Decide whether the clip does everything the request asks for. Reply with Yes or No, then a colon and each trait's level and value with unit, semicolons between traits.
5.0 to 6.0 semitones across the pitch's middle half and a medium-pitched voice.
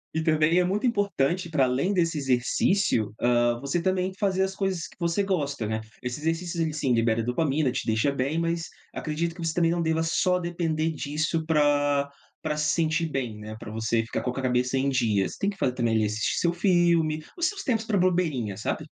Yes: wide, 5.5 semitones; medium, 155 Hz